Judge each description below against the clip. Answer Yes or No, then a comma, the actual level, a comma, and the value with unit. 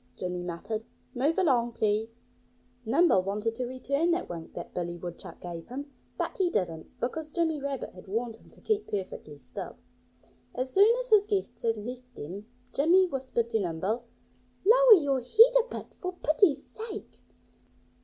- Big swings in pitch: Yes, wide, 8.9 semitones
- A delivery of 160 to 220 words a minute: Yes, average, 165 wpm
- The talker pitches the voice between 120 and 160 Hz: No, very high, 250 Hz